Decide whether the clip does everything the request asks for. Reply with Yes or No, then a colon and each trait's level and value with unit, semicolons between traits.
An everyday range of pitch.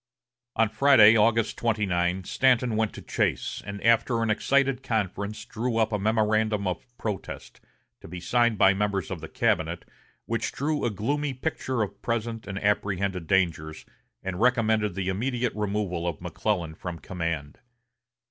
Yes: average, 3.4 semitones